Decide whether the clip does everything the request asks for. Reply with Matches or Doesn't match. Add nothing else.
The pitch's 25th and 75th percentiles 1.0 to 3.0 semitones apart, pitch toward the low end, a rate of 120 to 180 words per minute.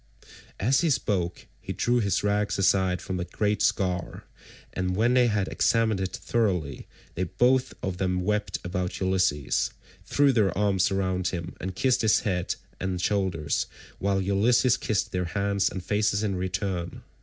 Matches